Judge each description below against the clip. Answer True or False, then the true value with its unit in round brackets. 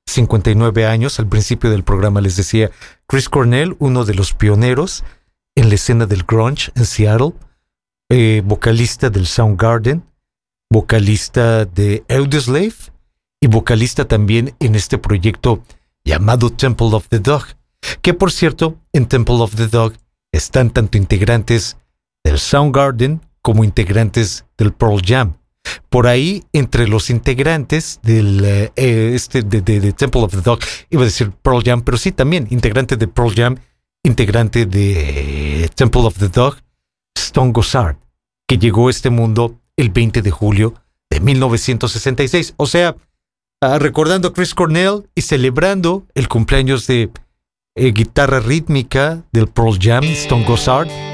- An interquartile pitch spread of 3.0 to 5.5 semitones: True (3.8 semitones)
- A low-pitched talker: True (120 Hz)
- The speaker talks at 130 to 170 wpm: True (140 wpm)